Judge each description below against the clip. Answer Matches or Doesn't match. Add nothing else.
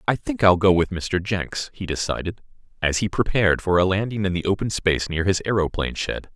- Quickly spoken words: Matches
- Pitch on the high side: Doesn't match